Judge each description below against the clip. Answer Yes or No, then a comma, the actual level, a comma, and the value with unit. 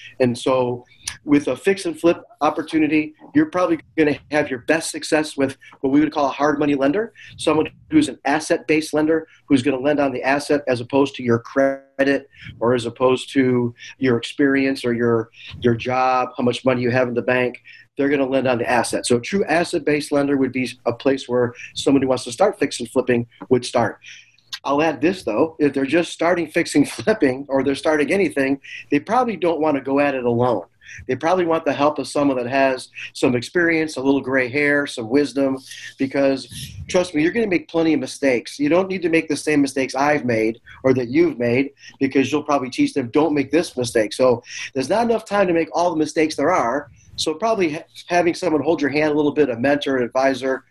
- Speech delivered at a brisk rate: Yes, fast, 220 wpm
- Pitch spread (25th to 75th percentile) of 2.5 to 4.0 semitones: Yes, average, 3.5 semitones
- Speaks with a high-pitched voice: No, medium, 140 Hz